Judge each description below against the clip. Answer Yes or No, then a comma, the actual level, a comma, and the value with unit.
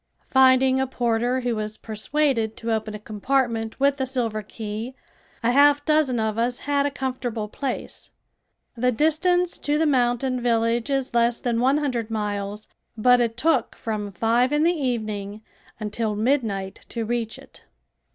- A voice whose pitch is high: Yes, high, 240 Hz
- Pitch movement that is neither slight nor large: Yes, average, 3.4 semitones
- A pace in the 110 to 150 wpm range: No, average, 160 wpm